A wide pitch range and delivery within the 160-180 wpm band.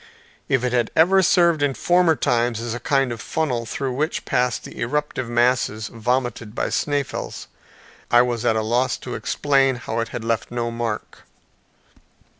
No: average, 3.3 semitones; average, 170 wpm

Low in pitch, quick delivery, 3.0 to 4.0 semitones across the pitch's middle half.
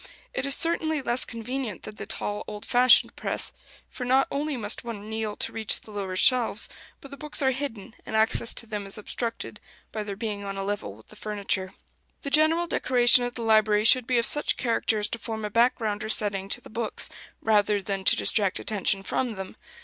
No: high, 220 Hz; fast, 210 wpm; average, 3.3 semitones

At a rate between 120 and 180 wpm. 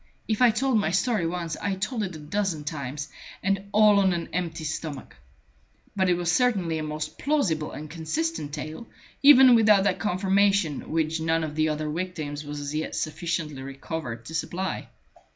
Yes: average, 175 wpm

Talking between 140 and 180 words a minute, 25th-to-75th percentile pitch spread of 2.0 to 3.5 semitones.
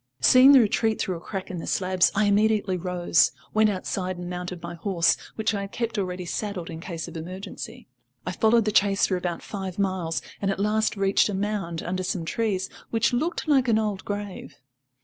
No: fast, 205 wpm; average, 3.0 semitones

